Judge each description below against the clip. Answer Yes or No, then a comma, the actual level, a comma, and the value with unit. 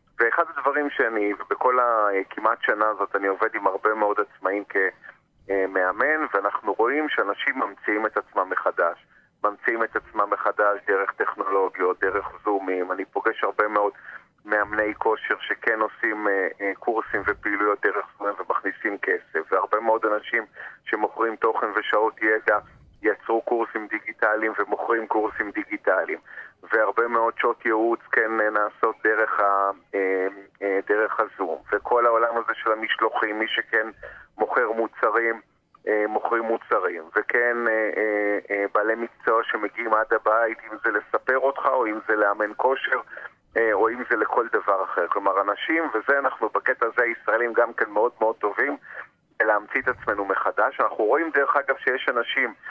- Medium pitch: No, low, 110 Hz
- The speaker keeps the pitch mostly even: Yes, narrow, 2.2 semitones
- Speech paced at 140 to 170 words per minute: Yes, average, 145 wpm